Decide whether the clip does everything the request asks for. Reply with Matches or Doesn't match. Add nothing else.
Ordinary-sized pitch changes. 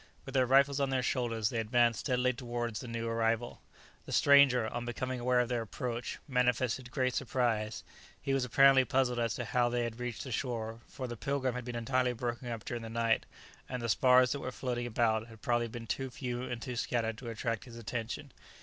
Doesn't match